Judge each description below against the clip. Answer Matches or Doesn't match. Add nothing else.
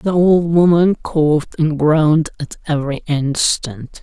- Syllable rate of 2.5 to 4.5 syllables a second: Matches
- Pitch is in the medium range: Matches